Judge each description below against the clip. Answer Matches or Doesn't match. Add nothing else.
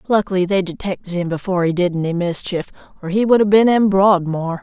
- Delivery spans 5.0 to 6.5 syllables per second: Matches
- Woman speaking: Matches